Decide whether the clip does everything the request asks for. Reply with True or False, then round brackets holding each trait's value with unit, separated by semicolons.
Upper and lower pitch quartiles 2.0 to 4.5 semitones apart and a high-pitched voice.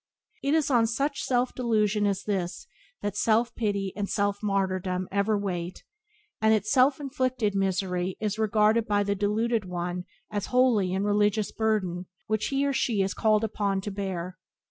True (2.7 semitones; 205 Hz)